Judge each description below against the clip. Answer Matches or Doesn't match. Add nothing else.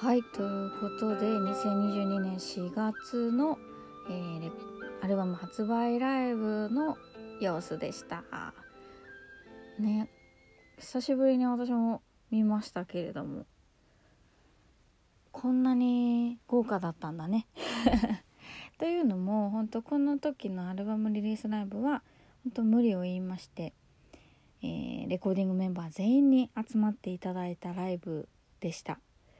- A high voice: Matches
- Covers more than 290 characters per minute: Doesn't match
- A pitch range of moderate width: Matches